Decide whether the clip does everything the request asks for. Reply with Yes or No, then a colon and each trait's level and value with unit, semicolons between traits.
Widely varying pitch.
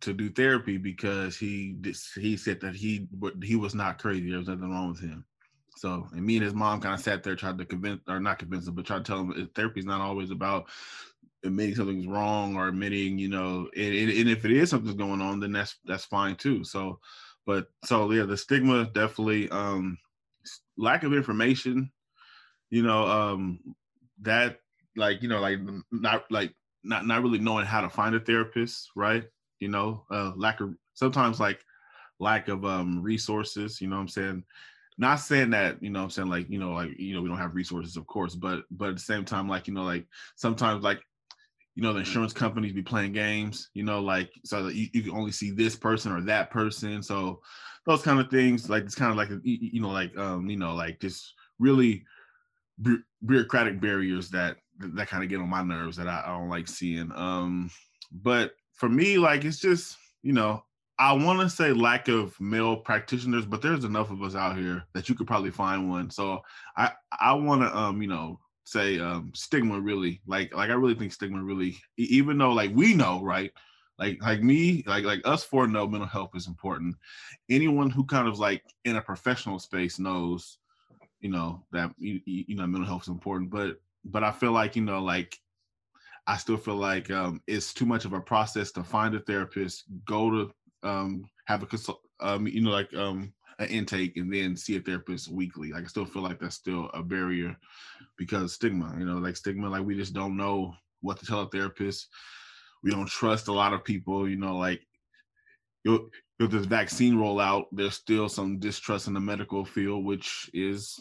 No: average, 3.0 semitones